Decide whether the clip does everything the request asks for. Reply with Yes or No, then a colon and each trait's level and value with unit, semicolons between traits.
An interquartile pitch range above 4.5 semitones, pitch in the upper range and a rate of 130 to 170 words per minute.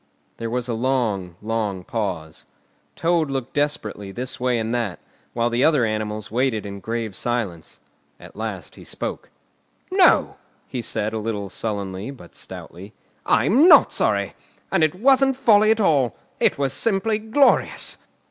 No: wide, 5.5 semitones; low, 120 Hz; average, 150 wpm